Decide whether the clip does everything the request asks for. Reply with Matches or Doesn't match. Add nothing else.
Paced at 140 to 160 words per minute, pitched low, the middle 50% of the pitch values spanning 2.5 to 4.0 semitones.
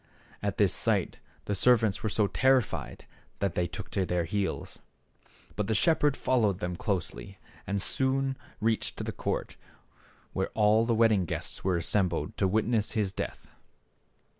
Matches